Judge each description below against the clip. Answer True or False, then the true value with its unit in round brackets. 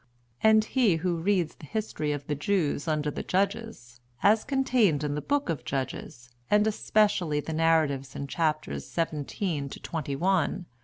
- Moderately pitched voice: True (165 Hz)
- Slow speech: False (155 wpm)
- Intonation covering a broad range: True (5.8 semitones)